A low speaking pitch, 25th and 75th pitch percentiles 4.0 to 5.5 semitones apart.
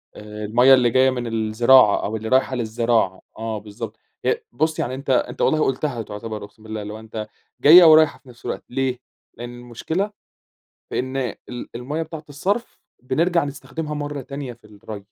Yes: low, 125 Hz; average, 4.5 semitones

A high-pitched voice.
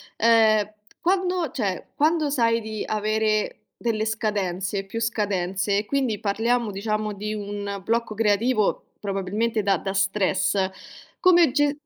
Yes: high, 215 Hz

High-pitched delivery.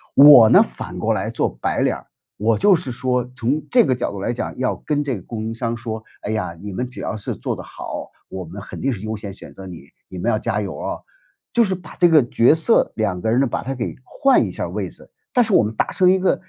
No: low, 120 Hz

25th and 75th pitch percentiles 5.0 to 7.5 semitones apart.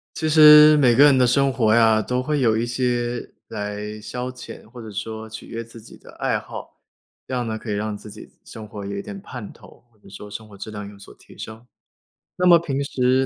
No: average, 3.4 semitones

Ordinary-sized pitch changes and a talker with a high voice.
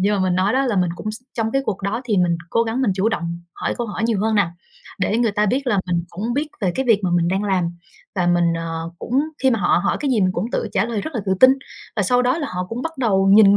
Yes: average, 4.5 semitones; high, 210 Hz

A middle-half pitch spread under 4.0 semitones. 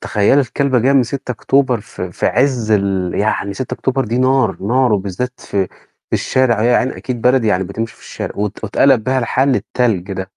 No: average, 4.3 semitones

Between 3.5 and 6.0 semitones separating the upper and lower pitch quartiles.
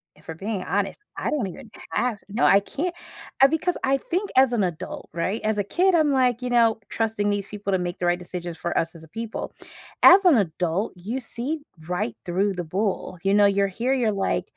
Yes: wide, 5.5 semitones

